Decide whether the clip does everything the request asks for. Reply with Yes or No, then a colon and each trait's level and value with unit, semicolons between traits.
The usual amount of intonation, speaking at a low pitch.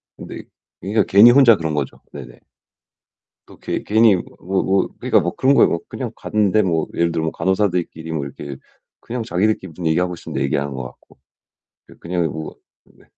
Yes: average, 4.6 semitones; very low, 90 Hz